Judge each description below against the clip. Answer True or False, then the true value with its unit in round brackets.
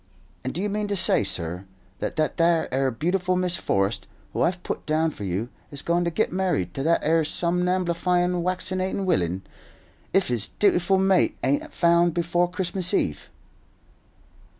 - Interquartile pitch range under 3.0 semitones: False (5.2 semitones)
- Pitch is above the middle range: False (170 Hz)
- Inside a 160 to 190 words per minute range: True (165 wpm)